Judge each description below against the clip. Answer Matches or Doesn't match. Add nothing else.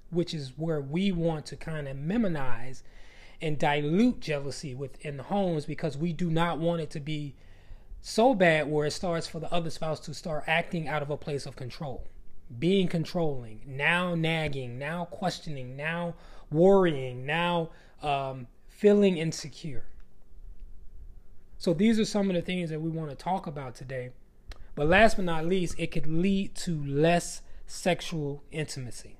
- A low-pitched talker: Doesn't match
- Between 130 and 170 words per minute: Matches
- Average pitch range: Matches